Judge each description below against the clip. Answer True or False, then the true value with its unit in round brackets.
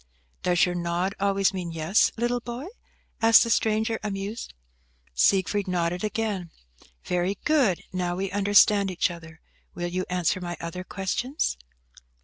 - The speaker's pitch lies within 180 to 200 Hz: True (190 Hz)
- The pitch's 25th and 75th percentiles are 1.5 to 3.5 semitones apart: True (3.2 semitones)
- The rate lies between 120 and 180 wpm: True (135 wpm)